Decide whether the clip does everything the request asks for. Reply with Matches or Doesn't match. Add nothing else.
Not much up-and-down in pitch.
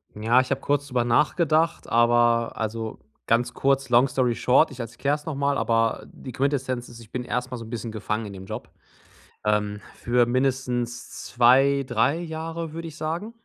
Doesn't match